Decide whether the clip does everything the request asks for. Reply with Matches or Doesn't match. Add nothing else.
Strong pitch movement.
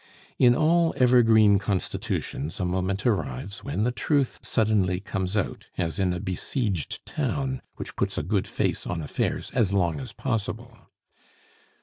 Doesn't match